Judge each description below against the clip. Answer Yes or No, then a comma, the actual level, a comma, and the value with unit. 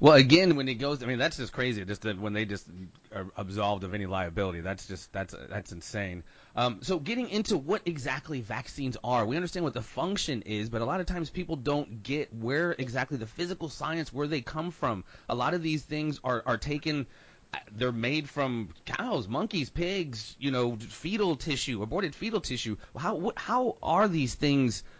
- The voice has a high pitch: No, low, 130 Hz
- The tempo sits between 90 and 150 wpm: No, average, 200 wpm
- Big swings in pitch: Yes, wide, 6.6 semitones